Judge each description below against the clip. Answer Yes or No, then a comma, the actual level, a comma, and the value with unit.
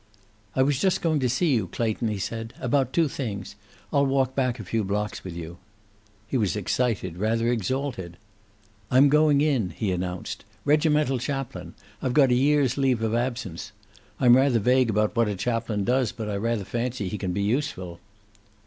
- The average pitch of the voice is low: Yes, low, 120 Hz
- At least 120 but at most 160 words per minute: No, average, 180 wpm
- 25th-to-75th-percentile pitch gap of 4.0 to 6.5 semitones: Yes, average, 4.4 semitones